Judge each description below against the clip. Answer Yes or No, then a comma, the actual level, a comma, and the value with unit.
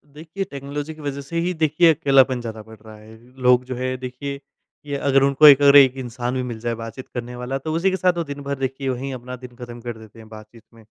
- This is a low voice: Yes, low, 130 Hz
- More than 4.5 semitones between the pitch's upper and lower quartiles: No, average, 2.9 semitones